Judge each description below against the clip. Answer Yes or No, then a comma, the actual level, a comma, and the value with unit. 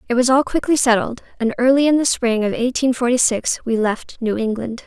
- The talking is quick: Yes, fast, 220 wpm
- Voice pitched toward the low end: No, high, 245 Hz